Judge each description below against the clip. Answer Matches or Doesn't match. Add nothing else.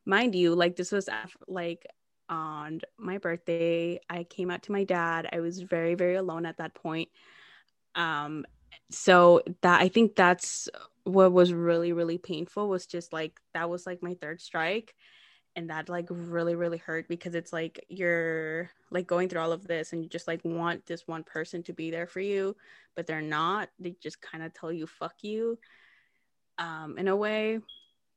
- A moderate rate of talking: Matches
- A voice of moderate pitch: Matches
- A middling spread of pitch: Doesn't match